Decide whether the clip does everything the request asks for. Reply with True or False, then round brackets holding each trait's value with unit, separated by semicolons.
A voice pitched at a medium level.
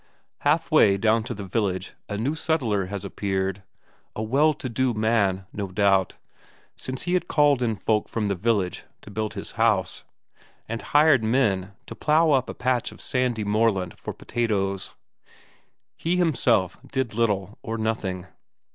False (110 Hz)